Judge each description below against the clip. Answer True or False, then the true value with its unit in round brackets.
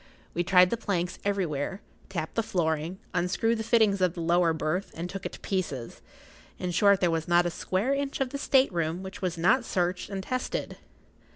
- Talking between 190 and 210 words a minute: True (195 wpm)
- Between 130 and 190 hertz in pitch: True (185 Hz)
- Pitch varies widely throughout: False (2.9 semitones)